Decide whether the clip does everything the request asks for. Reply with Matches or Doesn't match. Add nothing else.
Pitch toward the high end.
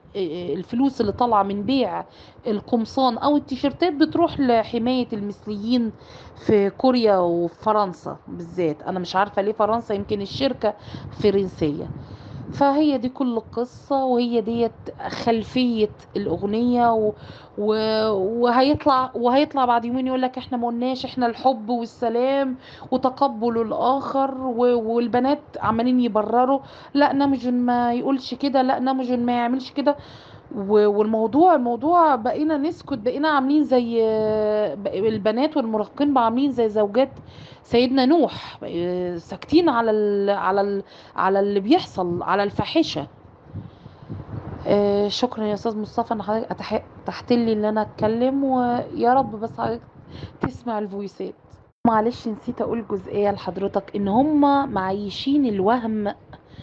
Matches